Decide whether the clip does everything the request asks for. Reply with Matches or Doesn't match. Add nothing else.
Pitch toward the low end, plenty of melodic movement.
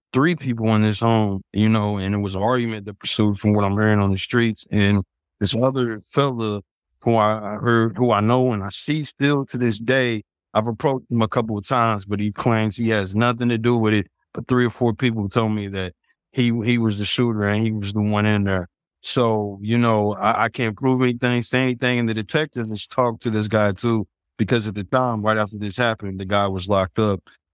Doesn't match